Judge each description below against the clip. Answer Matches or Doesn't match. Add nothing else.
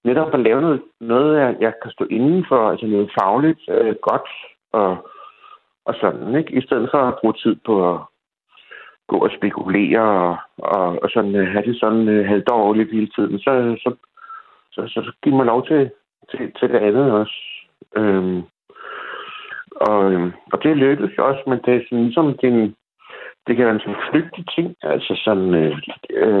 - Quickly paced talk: Doesn't match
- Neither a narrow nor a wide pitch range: Doesn't match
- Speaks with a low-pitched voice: Matches